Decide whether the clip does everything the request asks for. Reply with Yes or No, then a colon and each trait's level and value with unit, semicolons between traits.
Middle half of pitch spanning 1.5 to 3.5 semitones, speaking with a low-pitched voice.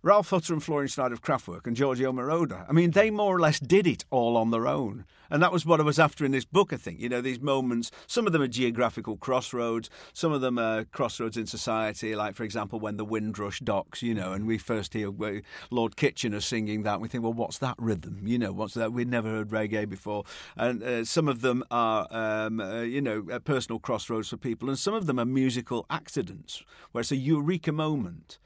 No: average, 4.2 semitones; low, 120 Hz